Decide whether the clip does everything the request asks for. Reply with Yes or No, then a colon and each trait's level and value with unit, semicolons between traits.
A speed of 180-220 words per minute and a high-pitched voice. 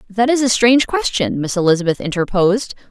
No: average, 165 wpm; high, 215 Hz